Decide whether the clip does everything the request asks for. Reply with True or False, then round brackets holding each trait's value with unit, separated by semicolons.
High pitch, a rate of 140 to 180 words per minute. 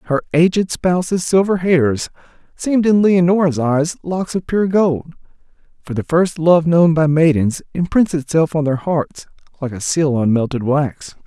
False (160 Hz; 165 wpm)